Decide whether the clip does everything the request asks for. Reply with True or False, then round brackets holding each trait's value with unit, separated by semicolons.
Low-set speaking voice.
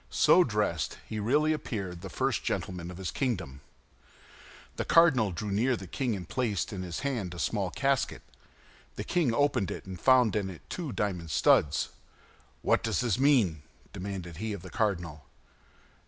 True (105 Hz)